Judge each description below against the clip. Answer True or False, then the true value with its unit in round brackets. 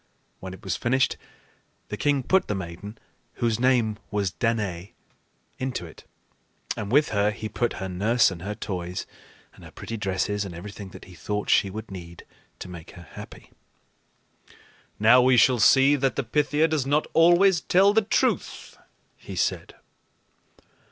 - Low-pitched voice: True (110 Hz)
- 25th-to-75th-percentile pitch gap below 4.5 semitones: False (5.6 semitones)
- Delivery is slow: False (160 wpm)